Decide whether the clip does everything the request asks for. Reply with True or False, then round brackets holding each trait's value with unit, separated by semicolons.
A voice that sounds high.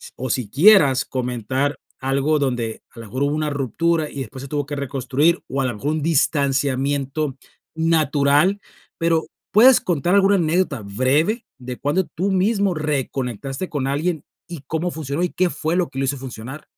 False (145 Hz)